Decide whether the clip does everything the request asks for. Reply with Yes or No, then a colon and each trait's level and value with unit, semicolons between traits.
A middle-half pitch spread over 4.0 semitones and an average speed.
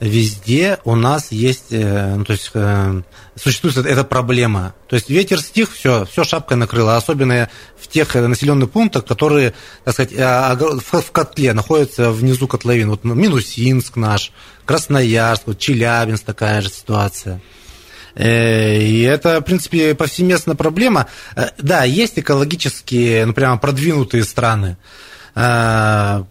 Yes: average, 4.7 semitones; average, 120 wpm